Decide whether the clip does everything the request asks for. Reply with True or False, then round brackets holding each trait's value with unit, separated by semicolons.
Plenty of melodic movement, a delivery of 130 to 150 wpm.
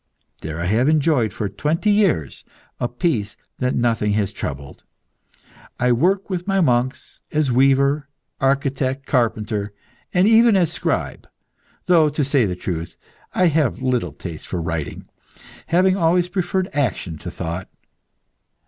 True (8.2 semitones; 140 wpm)